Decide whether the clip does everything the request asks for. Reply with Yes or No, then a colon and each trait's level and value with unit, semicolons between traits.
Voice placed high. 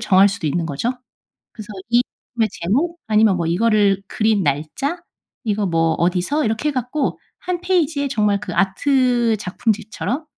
Yes: high, 215 Hz